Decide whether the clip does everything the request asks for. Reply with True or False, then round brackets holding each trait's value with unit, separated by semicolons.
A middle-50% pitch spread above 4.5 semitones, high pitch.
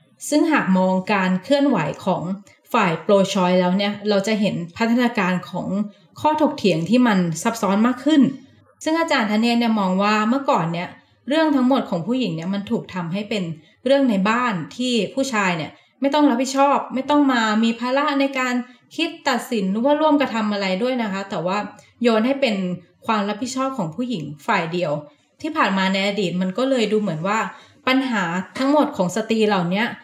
True (5.5 semitones; 220 Hz)